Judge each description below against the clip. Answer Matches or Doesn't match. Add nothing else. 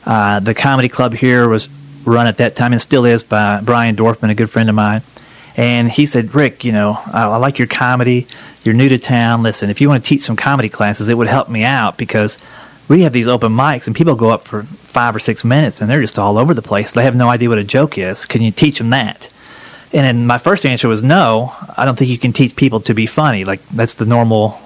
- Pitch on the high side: Doesn't match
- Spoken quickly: Matches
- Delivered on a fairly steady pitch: Doesn't match